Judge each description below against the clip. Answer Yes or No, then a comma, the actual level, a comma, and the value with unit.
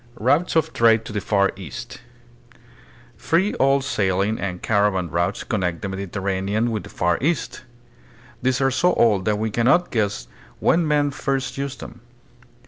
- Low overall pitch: Yes, low, 110 Hz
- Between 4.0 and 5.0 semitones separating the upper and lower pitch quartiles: No, wide, 5.6 semitones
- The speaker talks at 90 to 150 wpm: No, average, 165 wpm